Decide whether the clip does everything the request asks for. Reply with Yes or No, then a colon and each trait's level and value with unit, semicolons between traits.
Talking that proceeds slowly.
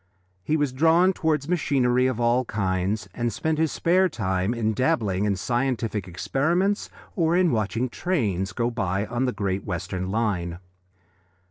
No: average, 150 wpm